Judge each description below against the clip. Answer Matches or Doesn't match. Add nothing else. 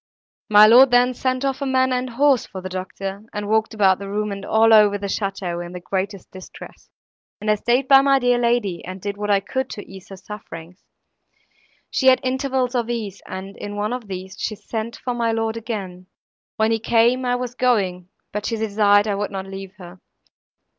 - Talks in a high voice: Matches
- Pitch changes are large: Doesn't match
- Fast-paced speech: Matches